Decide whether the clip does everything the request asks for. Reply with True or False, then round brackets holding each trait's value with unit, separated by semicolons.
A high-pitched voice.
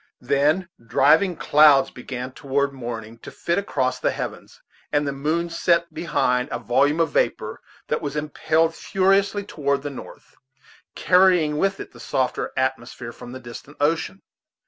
False (145 Hz)